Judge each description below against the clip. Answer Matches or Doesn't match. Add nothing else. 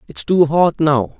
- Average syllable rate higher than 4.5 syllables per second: Doesn't match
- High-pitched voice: Doesn't match